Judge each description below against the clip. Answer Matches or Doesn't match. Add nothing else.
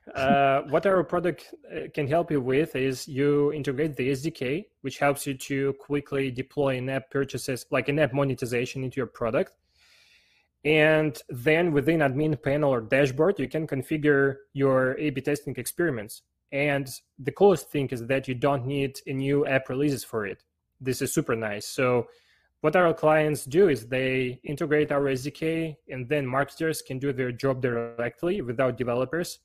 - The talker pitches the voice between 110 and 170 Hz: Matches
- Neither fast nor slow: Matches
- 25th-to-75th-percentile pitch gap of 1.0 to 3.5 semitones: Matches